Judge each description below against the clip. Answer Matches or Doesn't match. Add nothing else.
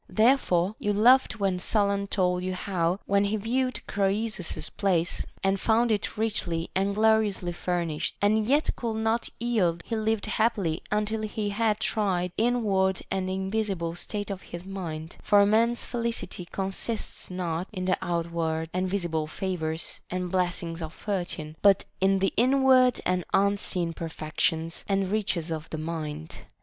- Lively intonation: Doesn't match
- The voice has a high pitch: Matches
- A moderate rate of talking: Matches